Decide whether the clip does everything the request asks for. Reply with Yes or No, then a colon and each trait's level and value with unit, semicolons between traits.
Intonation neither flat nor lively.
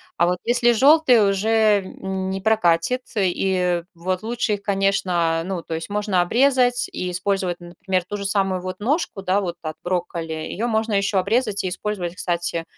Yes: average, 3.4 semitones